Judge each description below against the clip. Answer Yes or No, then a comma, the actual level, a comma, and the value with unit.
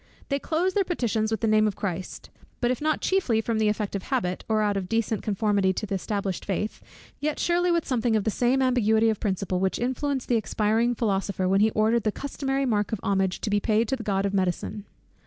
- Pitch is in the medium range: No, high, 220 Hz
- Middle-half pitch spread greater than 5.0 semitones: No, average, 3.7 semitones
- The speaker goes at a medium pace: No, fast, 230 wpm